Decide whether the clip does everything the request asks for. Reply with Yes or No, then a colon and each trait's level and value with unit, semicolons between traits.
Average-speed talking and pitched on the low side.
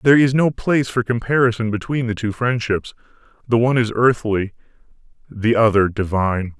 Yes: average, 155 wpm; low, 115 Hz